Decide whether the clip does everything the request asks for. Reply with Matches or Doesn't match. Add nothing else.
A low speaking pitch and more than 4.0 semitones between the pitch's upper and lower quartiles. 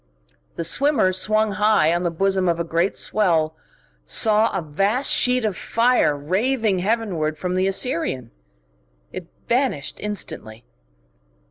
Doesn't match